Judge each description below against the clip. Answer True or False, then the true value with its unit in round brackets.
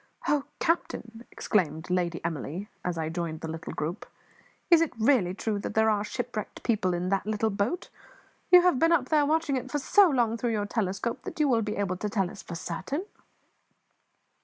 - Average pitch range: False (6.4 semitones)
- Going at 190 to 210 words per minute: True (195 wpm)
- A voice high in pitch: True (215 Hz)